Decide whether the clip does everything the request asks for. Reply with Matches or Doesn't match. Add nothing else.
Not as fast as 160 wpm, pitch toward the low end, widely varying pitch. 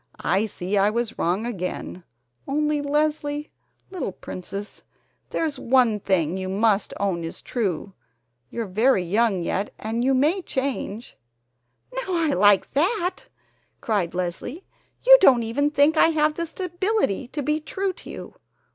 Doesn't match